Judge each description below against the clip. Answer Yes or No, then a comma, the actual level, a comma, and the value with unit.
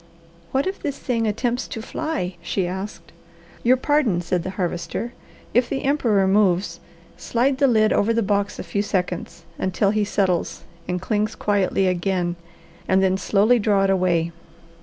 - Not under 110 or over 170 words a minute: Yes, average, 160 wpm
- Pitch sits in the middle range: No, high, 200 Hz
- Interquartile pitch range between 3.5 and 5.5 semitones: Yes, average, 3.9 semitones